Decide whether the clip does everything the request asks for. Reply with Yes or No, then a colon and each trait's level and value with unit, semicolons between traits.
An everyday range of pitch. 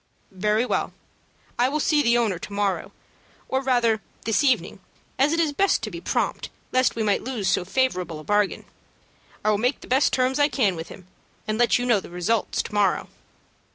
Yes: average, 4.4 semitones